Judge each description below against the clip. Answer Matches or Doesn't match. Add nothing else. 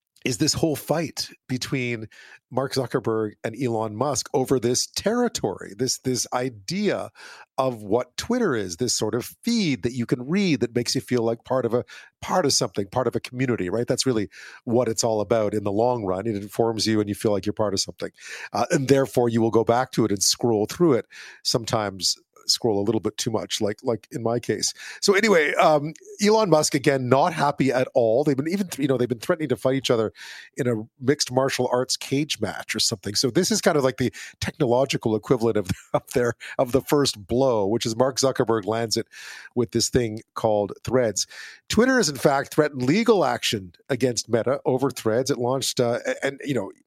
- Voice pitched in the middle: Doesn't match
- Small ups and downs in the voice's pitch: Doesn't match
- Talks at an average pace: Doesn't match